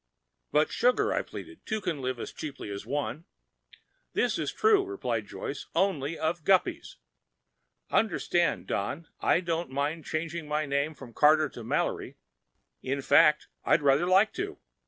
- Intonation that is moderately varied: Yes, average, 4.7 semitones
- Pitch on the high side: No, medium, 155 Hz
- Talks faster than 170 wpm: No, average, 150 wpm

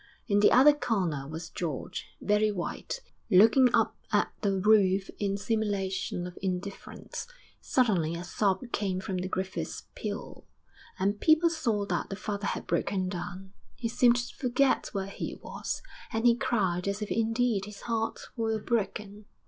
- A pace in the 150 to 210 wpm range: Yes, average, 155 wpm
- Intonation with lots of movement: No, average, 3.3 semitones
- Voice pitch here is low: No, high, 205 Hz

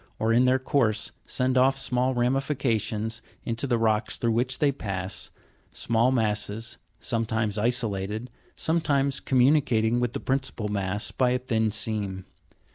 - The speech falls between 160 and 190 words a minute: No, average, 150 wpm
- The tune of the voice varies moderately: Yes, average, 3.1 semitones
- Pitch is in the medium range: No, low, 115 Hz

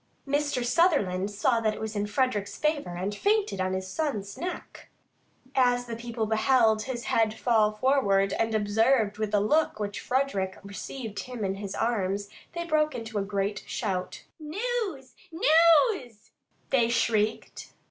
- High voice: Yes, high, 225 Hz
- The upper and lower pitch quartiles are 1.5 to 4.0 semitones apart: No, average, 4.6 semitones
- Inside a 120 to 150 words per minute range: Yes, average, 145 wpm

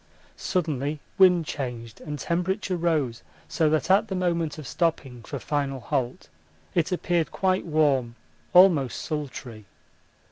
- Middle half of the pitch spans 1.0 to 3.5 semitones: No, average, 4.8 semitones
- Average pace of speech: No, slow, 130 wpm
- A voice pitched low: No, medium, 155 Hz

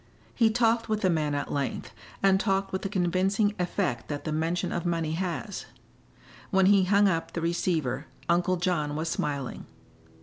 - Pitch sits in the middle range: Yes, medium, 175 Hz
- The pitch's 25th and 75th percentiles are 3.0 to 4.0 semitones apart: Yes, average, 3.7 semitones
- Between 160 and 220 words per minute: Yes, average, 170 wpm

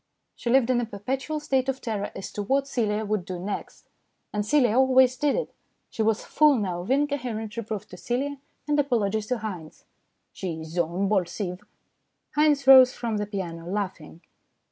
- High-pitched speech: Yes, high, 220 Hz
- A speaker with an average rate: Yes, average, 180 wpm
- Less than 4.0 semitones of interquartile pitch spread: No, average, 5.0 semitones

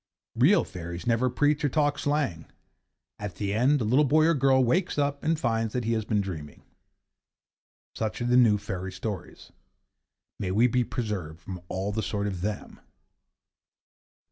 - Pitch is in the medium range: No, low, 115 Hz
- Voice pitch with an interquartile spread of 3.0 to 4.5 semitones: No, wide, 5.6 semitones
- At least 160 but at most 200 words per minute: Yes, average, 170 wpm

